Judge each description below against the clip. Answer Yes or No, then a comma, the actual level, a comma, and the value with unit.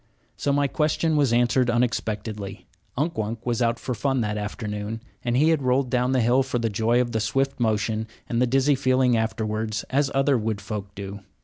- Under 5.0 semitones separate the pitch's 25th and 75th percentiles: Yes, average, 3.4 semitones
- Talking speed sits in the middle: Yes, average, 195 wpm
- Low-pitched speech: Yes, low, 120 Hz